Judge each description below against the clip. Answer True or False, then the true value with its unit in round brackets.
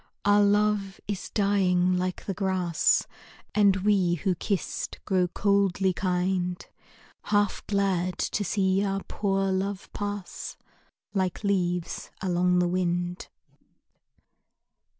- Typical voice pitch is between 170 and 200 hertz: True (190 Hz)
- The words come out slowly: True (110 wpm)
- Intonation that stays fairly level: True (1.9 semitones)